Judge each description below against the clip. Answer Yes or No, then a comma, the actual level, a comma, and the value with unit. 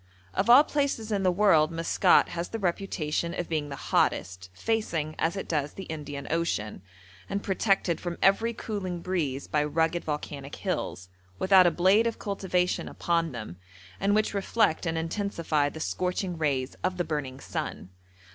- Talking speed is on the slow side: No, average, 165 wpm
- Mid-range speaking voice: Yes, medium, 170 Hz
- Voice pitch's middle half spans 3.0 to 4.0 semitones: No, average, 4.5 semitones